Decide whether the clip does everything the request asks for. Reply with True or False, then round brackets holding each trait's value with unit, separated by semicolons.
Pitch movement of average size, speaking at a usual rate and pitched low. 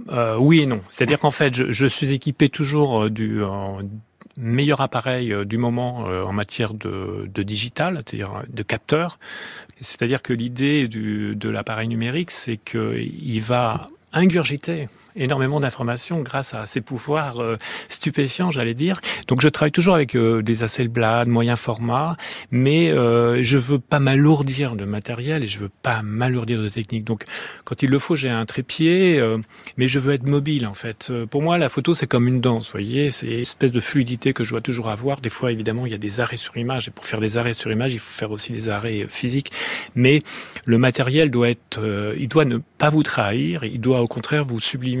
True (4.0 semitones; 195 wpm; 125 Hz)